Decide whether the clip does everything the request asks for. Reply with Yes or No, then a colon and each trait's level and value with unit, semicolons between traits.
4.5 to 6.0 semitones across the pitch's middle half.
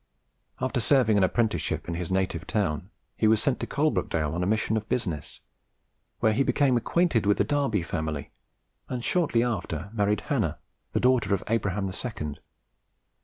Yes: wide, 5.5 semitones